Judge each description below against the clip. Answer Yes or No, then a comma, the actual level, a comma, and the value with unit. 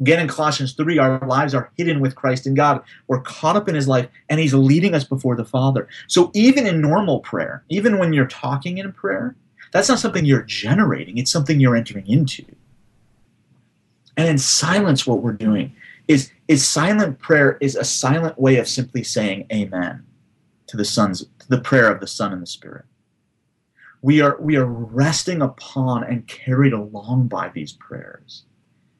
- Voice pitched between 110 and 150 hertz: Yes, low, 135 Hz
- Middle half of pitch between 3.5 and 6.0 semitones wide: Yes, average, 4.0 semitones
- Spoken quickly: No, average, 185 wpm